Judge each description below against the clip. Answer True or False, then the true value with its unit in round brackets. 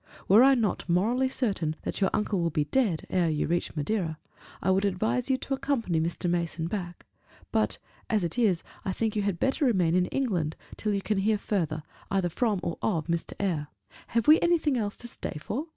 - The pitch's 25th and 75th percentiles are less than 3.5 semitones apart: False (5.2 semitones)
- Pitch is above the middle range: True (195 Hz)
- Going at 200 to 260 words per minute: True (205 wpm)